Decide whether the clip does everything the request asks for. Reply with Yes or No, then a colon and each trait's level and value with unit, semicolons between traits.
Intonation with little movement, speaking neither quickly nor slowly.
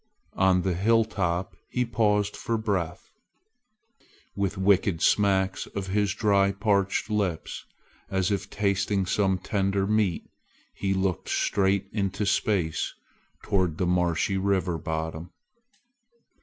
No: narrow, 1.9 semitones; slow, 115 wpm